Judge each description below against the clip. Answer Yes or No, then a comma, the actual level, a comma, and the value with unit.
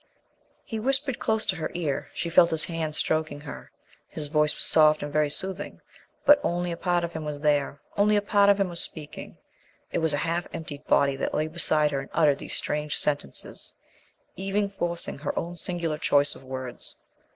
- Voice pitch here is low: No, medium, 160 Hz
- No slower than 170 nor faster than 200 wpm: Yes, average, 195 wpm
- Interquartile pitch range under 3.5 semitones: Yes, average, 3.1 semitones